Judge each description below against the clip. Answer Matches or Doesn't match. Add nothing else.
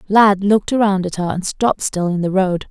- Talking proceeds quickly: Matches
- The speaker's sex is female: Matches